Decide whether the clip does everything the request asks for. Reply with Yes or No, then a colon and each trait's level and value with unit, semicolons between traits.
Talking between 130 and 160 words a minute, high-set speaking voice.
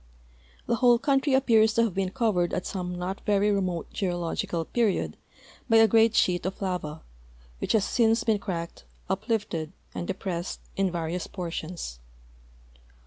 Yes: average, 145 wpm; high, 195 Hz